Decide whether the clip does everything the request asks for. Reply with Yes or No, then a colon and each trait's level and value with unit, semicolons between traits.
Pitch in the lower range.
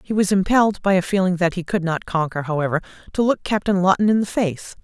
No: medium, 185 Hz